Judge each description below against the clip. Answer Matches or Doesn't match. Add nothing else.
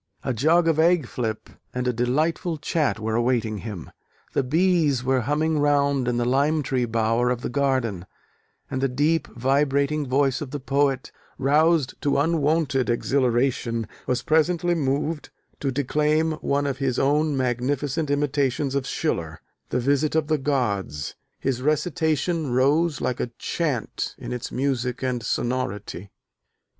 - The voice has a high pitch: Doesn't match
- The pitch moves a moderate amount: Matches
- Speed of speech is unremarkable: Matches